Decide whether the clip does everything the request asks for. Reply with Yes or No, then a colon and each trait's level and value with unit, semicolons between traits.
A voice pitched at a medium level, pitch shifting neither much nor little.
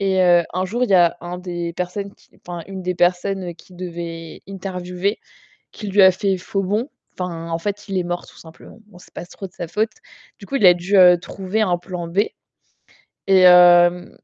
No: medium, 180 Hz; narrow, 2.0 semitones